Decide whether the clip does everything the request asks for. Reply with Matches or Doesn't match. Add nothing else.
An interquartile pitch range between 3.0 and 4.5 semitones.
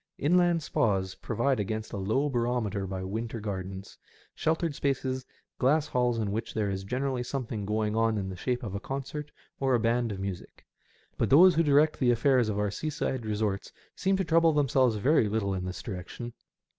Doesn't match